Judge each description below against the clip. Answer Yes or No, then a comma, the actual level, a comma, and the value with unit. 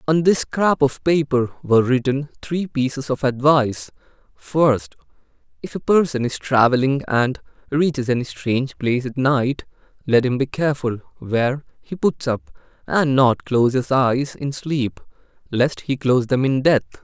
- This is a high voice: No, low, 135 Hz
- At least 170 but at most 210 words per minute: No, average, 155 wpm